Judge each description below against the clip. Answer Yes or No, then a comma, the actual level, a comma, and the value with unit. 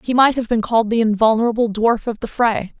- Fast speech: Yes, fast, 235 wpm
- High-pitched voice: Yes, high, 225 Hz